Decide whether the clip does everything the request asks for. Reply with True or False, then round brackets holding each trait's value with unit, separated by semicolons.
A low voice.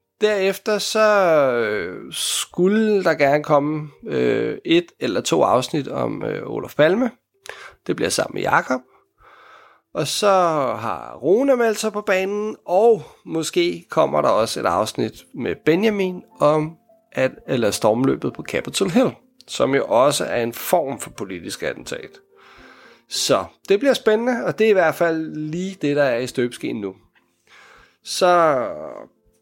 False (210 Hz)